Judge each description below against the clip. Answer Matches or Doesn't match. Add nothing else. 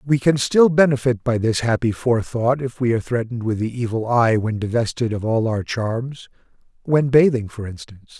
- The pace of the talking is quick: Doesn't match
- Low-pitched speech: Matches